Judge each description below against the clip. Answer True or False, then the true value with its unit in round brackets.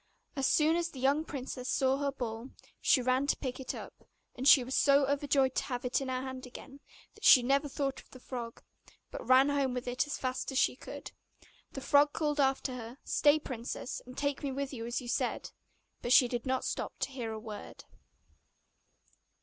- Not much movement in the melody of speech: True (2.0 semitones)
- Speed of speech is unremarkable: False (210 wpm)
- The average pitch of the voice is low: False (265 Hz)